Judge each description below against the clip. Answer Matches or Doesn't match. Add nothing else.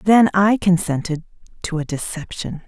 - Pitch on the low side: Doesn't match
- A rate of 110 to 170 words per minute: Matches